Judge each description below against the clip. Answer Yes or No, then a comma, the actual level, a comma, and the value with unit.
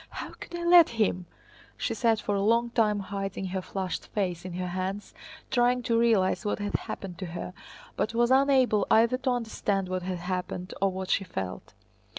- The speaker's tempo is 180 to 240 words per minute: Yes, average, 190 wpm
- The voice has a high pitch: Yes, high, 200 Hz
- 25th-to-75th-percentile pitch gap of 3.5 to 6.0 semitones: Yes, average, 4.0 semitones